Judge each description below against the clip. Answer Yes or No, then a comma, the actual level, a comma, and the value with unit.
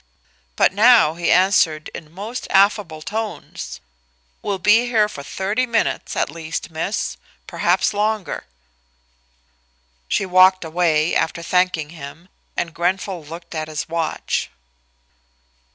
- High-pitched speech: No, medium, 180 Hz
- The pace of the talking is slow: Yes, slow, 120 wpm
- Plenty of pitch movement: No, average, 4.2 semitones